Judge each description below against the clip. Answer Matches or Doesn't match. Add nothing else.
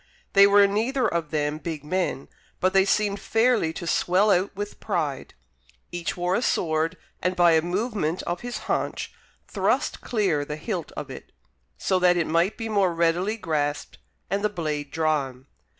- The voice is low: Doesn't match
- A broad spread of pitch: Doesn't match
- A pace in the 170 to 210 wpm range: Matches